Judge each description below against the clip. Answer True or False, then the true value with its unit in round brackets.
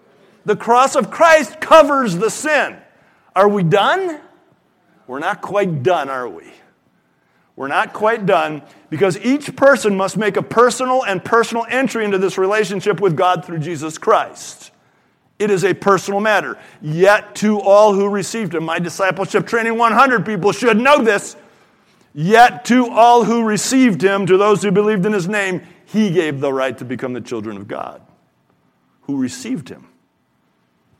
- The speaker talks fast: False (160 wpm)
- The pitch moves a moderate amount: True (4.2 semitones)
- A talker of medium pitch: False (205 Hz)